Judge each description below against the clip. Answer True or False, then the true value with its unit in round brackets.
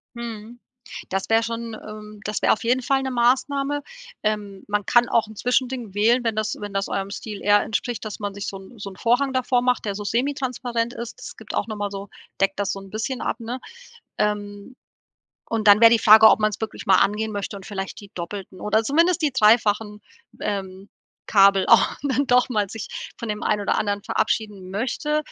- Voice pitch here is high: True (215 Hz)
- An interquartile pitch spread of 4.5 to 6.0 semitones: False (3.0 semitones)